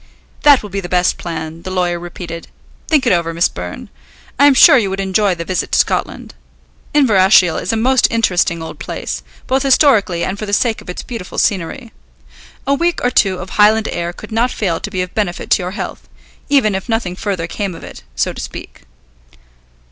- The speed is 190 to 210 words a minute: Yes, fast, 205 wpm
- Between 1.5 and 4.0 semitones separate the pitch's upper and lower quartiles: No, average, 4.4 semitones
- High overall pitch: Yes, high, 195 Hz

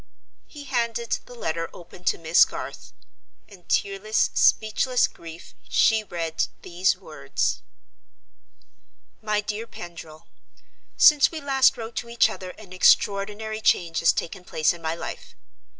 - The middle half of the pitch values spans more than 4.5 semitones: Yes, average, 5.3 semitones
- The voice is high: Yes, high, 205 Hz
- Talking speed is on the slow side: Yes, slow, 130 wpm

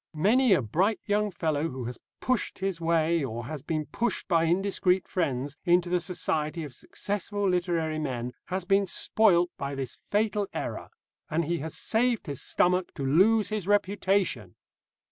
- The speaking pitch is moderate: Yes, medium, 175 Hz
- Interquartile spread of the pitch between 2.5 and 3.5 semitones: No, average, 4.5 semitones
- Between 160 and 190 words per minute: Yes, average, 165 wpm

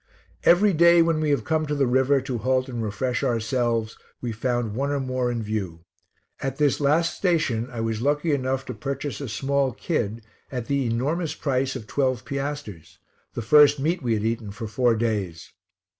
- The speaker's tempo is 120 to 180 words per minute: No, average, 190 wpm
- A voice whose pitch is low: Yes, low, 130 Hz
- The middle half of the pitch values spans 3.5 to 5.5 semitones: Yes, average, 4.0 semitones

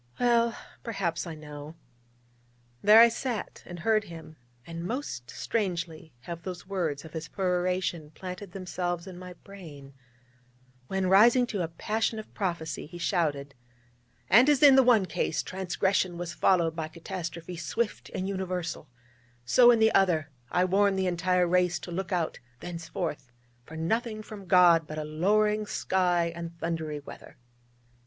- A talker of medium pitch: Yes, medium, 180 Hz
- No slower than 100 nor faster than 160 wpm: Yes, average, 150 wpm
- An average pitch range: Yes, average, 3.3 semitones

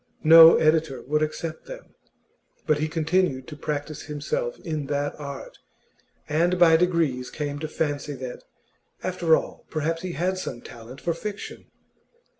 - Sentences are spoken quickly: No, average, 145 wpm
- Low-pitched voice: No, medium, 155 Hz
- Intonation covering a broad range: No, average, 2.7 semitones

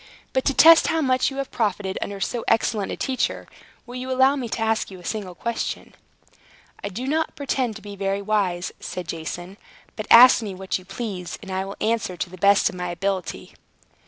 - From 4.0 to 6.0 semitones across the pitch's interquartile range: Yes, average, 4.8 semitones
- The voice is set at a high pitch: Yes, high, 210 Hz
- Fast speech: Yes, fast, 210 wpm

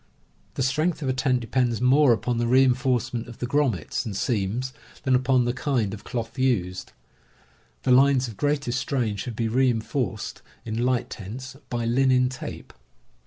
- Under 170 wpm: No, average, 180 wpm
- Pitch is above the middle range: No, low, 125 Hz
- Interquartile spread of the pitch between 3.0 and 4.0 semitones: No, narrow, 2.4 semitones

